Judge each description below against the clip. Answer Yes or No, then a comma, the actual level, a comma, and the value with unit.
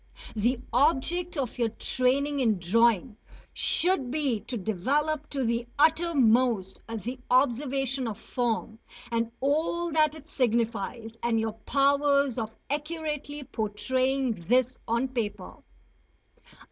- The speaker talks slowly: Yes, slow, 115 wpm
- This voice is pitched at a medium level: No, very high, 255 Hz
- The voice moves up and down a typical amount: Yes, average, 4.0 semitones